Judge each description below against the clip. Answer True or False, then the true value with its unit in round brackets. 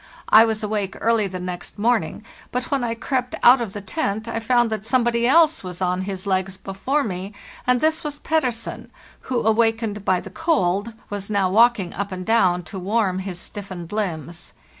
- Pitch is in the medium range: False (215 Hz)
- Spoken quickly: False (185 wpm)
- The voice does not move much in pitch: False (4.1 semitones)